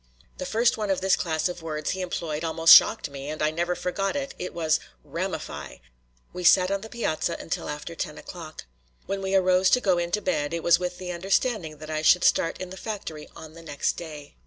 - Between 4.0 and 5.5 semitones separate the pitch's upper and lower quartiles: No, average, 3.3 semitones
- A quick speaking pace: Yes, fast, 220 wpm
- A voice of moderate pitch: Yes, medium, 175 Hz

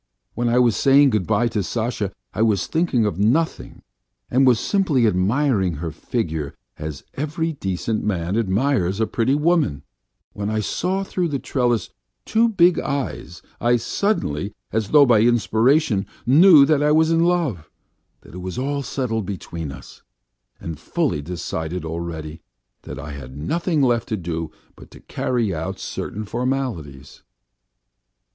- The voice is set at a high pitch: No, low, 115 Hz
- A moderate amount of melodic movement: No, wide, 7.9 semitones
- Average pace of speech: Yes, average, 150 wpm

